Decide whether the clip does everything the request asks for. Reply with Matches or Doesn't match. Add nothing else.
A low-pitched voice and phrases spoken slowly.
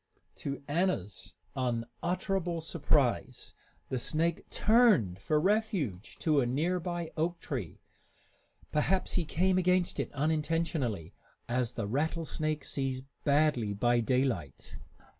Doesn't match